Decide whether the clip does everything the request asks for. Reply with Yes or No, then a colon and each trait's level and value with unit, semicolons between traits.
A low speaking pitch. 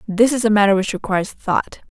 No: high, 210 Hz